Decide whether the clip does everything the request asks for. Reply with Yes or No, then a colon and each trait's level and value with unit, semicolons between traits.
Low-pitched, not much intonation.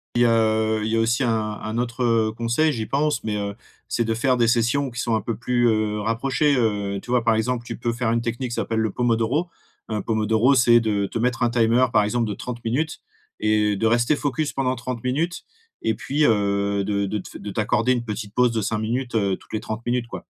Yes: low, 115 Hz; narrow, 2.2 semitones